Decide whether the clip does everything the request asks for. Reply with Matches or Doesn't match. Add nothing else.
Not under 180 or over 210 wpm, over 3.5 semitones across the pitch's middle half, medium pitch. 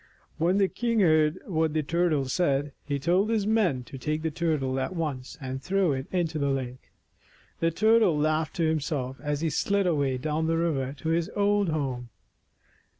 Matches